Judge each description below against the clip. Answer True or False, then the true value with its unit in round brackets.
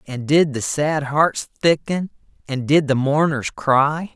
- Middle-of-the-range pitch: True (145 Hz)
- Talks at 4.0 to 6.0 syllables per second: False (3.7 syllables/s)